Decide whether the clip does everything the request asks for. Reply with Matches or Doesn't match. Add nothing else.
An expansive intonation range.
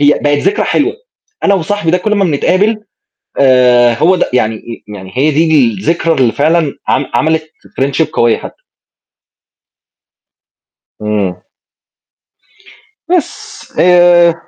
Matches